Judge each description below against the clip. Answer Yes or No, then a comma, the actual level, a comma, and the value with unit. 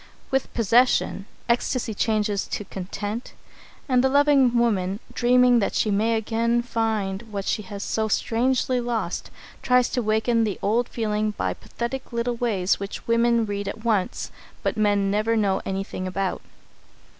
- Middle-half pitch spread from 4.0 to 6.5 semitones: No, average, 2.8 semitones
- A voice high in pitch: Yes, high, 225 Hz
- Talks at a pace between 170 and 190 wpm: No, average, 150 wpm